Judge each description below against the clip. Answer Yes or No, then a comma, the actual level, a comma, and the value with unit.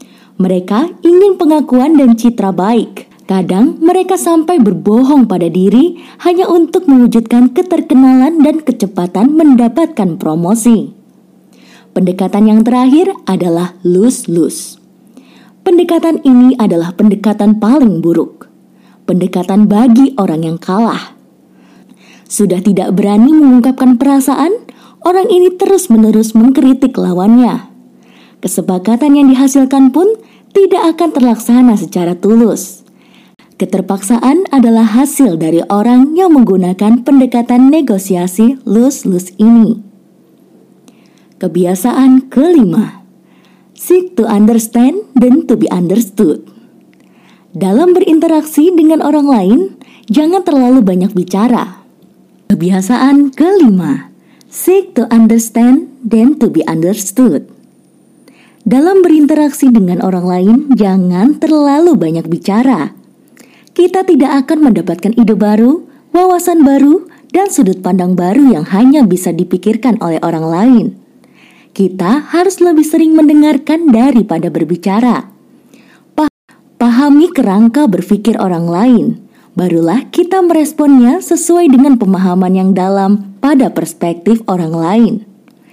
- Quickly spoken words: No, average, 100 wpm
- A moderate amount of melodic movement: No, wide, 6.5 semitones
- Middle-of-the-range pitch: No, high, 240 Hz